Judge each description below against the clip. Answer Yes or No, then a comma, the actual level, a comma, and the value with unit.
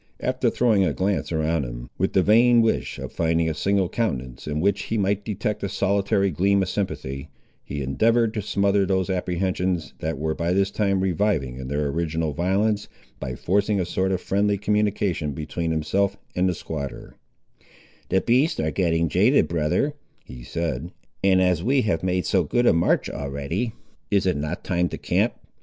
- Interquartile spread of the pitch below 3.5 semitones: No, average, 4.2 semitones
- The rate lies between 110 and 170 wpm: No, average, 180 wpm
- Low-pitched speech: Yes, very low, 90 Hz